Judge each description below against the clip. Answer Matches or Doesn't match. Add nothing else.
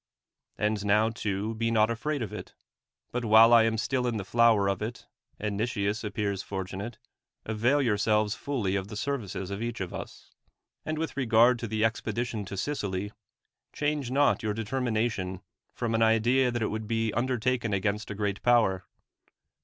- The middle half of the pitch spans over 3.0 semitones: Doesn't match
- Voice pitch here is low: Matches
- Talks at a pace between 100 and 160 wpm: Doesn't match